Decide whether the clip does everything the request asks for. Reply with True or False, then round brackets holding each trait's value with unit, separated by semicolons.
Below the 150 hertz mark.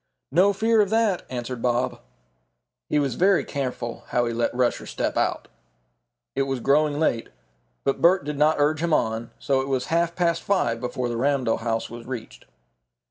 True (135 Hz)